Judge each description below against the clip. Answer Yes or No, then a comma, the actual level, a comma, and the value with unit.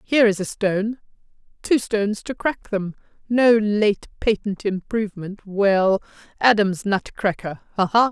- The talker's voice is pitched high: Yes, high, 205 Hz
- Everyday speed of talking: No, slow, 120 wpm